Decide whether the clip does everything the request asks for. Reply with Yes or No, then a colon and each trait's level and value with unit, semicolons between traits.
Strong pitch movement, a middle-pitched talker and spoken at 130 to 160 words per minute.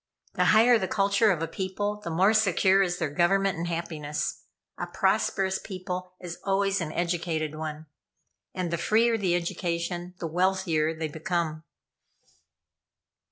No: average, 2.9 semitones; medium, 180 Hz; average, 145 wpm